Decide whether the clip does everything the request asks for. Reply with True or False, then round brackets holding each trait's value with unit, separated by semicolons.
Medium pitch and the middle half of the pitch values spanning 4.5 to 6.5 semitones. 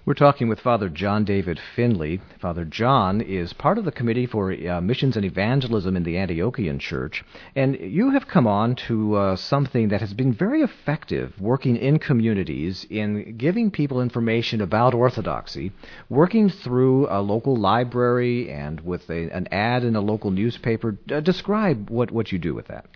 False (115 Hz; 5.1 semitones)